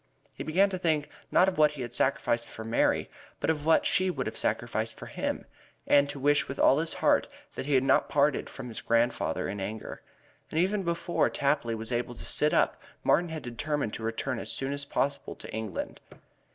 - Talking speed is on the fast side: Yes, fast, 210 wpm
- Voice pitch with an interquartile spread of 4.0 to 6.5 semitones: Yes, average, 4.6 semitones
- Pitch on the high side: No, medium, 140 Hz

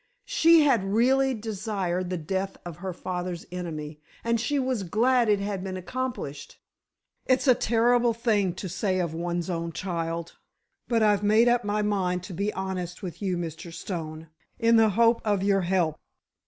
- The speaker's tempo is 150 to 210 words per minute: Yes, average, 170 wpm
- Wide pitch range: No, average, 4.6 semitones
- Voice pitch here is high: Yes, high, 195 Hz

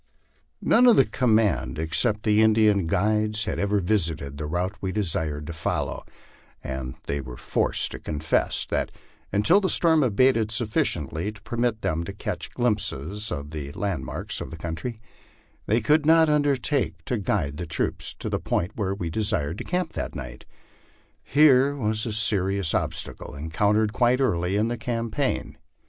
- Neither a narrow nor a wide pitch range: No, wide, 6.4 semitones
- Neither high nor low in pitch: No, low, 105 Hz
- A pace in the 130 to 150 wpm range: No, average, 165 wpm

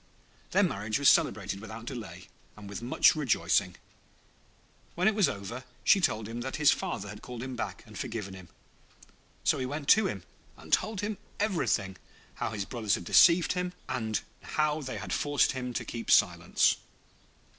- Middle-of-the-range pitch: No, low, 125 Hz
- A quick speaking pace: No, average, 175 wpm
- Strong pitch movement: Yes, wide, 6.4 semitones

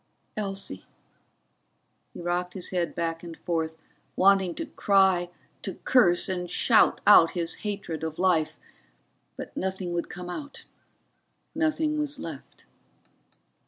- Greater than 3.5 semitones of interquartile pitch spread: No, narrow, 2.6 semitones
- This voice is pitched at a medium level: Yes, medium, 180 Hz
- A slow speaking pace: Yes, slow, 125 wpm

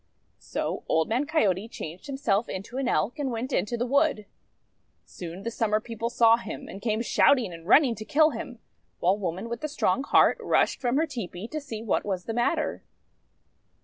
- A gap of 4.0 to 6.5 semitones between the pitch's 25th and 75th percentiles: Yes, average, 4.9 semitones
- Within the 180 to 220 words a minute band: Yes, average, 190 wpm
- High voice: Yes, high, 230 Hz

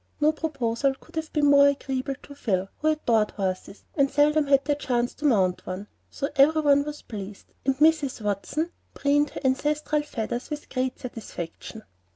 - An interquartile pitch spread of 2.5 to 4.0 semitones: No, average, 4.5 semitones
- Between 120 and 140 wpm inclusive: No, average, 175 wpm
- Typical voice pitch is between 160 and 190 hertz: No, very high, 275 Hz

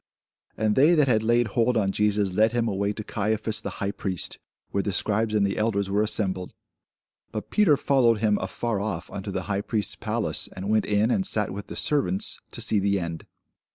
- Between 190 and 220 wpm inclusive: Yes, fast, 205 wpm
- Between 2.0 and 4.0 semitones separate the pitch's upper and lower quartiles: Yes, narrow, 2.4 semitones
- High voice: No, low, 105 Hz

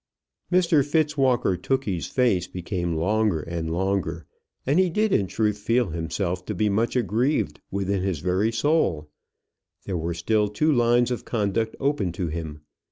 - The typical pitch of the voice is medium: No, low, 105 Hz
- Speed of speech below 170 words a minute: Yes, average, 155 wpm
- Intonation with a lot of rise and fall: Yes, wide, 6.1 semitones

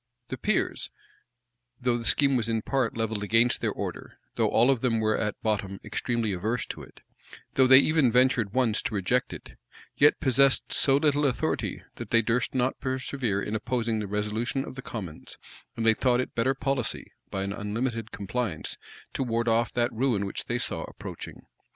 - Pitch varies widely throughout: No, average, 3.3 semitones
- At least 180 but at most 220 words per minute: Yes, average, 185 wpm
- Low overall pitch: Yes, low, 120 Hz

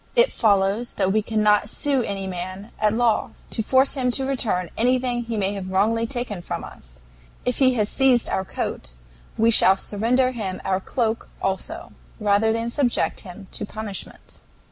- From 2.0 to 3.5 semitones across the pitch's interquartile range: No, average, 3.9 semitones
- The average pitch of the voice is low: No, high, 220 Hz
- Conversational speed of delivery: Yes, average, 170 wpm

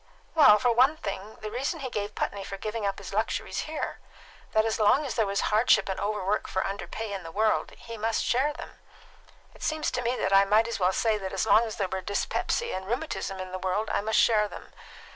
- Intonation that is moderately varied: Yes, average, 3.0 semitones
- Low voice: No, high, 215 Hz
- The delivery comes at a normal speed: No, fast, 235 wpm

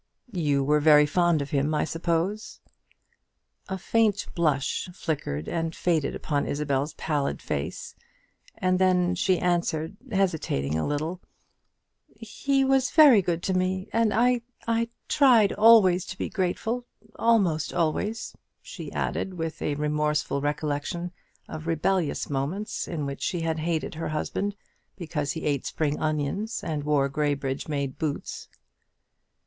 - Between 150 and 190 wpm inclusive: No, slow, 135 wpm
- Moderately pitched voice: Yes, medium, 165 Hz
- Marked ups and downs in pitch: No, average, 4.4 semitones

